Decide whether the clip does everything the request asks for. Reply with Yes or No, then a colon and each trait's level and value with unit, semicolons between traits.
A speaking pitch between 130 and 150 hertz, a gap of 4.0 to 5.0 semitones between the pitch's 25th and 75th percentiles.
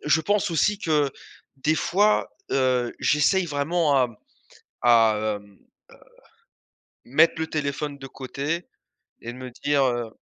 Yes: medium, 140 Hz; average, 4.5 semitones